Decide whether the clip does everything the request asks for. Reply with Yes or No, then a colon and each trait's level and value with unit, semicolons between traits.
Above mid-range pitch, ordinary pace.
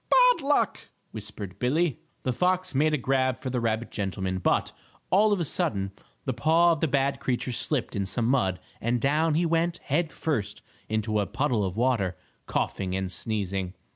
No: low, 125 Hz; average, 180 wpm